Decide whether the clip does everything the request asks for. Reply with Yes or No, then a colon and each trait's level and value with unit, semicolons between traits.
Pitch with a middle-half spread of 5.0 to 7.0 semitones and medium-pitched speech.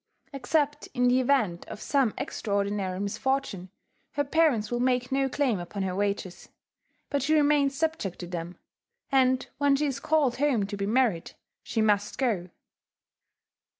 No: wide, 5.6 semitones; high, 245 Hz